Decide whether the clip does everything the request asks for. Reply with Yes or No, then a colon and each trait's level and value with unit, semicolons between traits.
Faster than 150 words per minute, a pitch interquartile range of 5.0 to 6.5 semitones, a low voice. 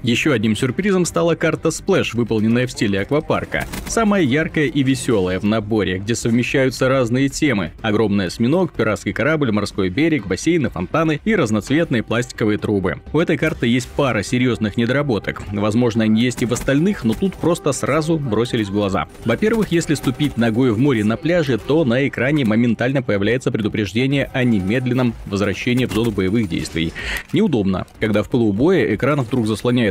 Yes: fast, 160 wpm; average, 5.3 semitones; low, 120 Hz